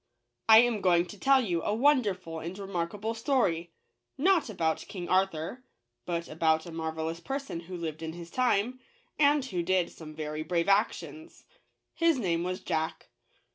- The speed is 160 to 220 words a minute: Yes, average, 170 wpm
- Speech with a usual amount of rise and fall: No, wide, 5.9 semitones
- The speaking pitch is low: No, medium, 180 Hz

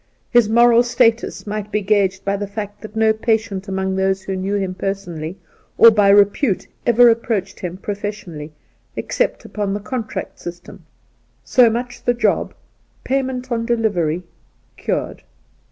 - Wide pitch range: No, average, 3.2 semitones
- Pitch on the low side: No, high, 205 Hz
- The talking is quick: No, average, 155 wpm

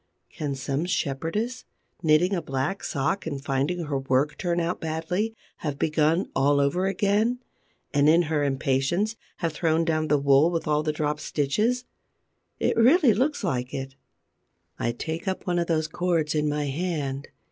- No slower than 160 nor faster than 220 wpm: Yes, average, 165 wpm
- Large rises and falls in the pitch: No, average, 4.1 semitones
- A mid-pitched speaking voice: Yes, medium, 155 Hz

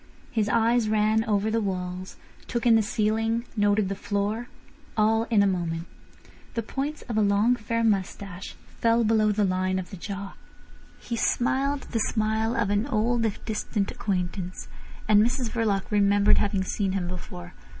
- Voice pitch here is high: Yes, high, 215 Hz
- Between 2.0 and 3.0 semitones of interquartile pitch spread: Yes, narrow, 2.5 semitones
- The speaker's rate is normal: Yes, average, 160 wpm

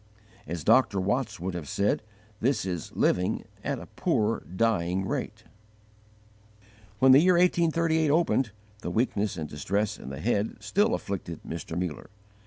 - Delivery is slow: No, average, 145 wpm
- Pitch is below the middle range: Yes, low, 105 Hz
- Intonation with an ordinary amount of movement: No, wide, 7.1 semitones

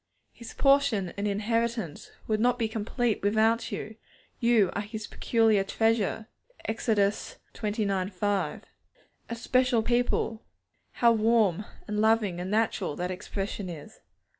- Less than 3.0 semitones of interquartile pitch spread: Yes, narrow, 2.4 semitones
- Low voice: No, high, 220 Hz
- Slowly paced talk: Yes, slow, 125 wpm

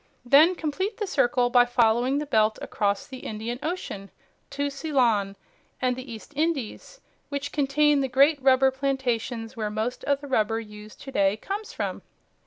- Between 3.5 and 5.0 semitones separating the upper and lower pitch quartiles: Yes, average, 4.2 semitones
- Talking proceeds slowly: No, average, 165 wpm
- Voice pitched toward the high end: Yes, very high, 260 Hz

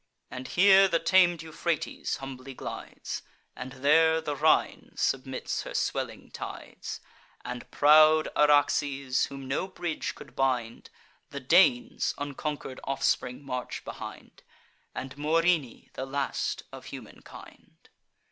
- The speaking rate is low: Yes, slow, 115 wpm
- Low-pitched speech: No, medium, 145 Hz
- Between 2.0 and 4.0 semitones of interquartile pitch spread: Yes, average, 3.6 semitones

